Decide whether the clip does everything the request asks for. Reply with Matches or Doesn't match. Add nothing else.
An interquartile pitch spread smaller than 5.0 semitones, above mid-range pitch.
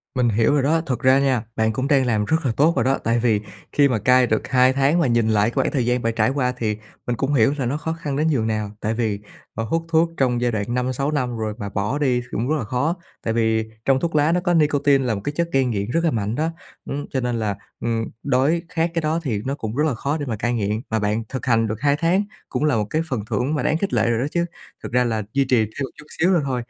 Doesn't match